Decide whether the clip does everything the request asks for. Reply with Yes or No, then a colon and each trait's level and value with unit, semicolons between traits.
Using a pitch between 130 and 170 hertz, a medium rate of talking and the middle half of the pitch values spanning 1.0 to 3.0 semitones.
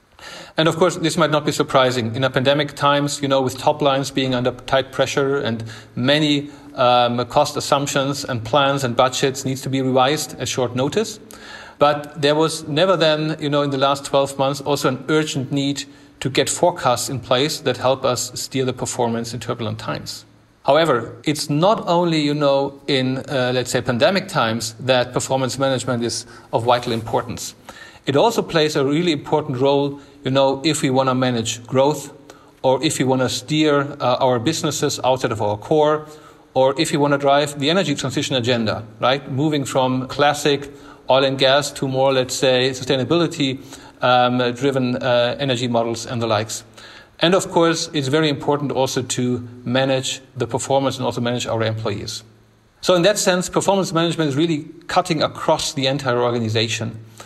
Yes: low, 135 Hz; average, 180 wpm; narrow, 2.6 semitones